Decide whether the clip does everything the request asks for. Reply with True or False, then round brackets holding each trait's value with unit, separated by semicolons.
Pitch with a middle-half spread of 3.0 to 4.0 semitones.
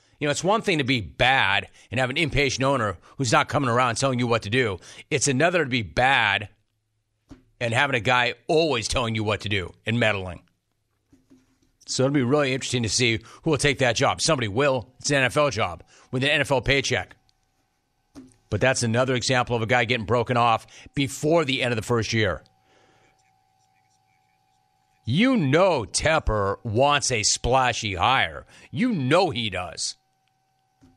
False (5.0 semitones)